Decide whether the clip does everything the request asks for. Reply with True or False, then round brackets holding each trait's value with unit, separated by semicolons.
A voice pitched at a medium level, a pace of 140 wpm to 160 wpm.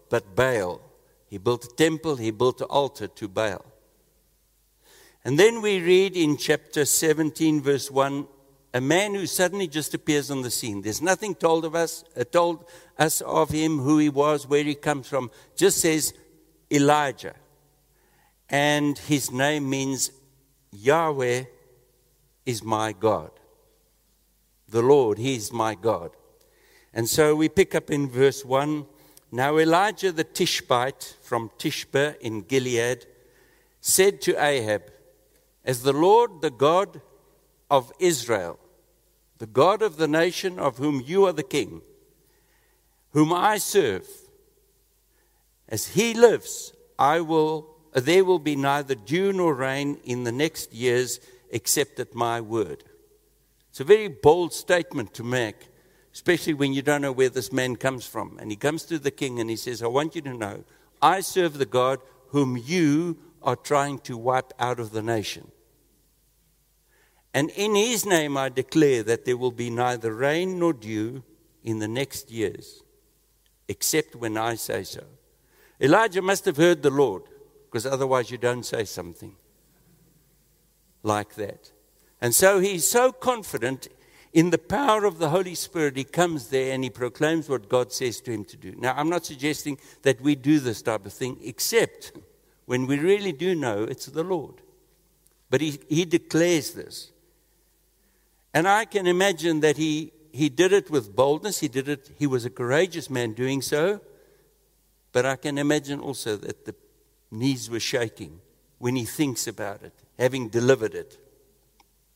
True (145 Hz; 155 wpm)